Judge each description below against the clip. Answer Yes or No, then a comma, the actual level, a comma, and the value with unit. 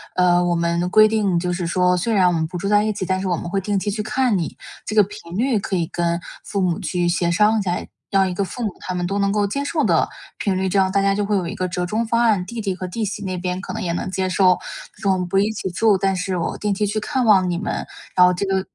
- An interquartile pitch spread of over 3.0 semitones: No, narrow, 2.6 semitones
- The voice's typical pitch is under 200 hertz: Yes, high, 190 Hz